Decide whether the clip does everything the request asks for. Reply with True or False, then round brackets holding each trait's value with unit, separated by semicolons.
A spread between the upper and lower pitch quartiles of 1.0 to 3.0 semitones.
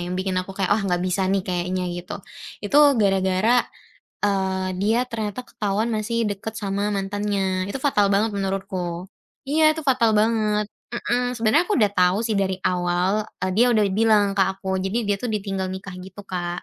True (2.7 semitones)